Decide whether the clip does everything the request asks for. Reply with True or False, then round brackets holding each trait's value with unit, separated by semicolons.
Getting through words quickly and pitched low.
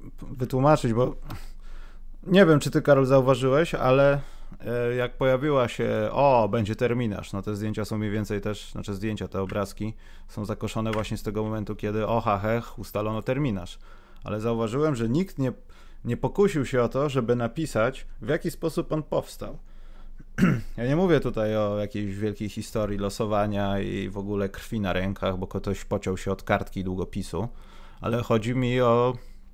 True (165 wpm; 110 Hz)